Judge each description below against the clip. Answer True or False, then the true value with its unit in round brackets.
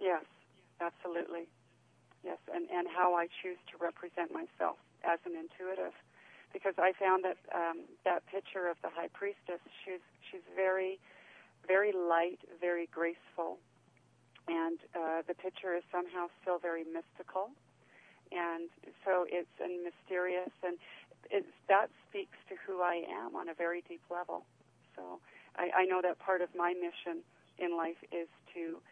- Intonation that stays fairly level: True (1.6 semitones)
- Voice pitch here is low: False (175 Hz)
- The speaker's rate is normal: True (150 wpm)